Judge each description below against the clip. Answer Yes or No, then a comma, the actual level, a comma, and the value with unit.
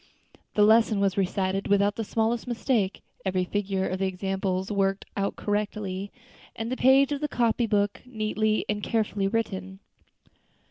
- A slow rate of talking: No, average, 150 wpm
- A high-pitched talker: Yes, high, 205 Hz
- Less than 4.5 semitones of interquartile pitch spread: Yes, narrow, 2.6 semitones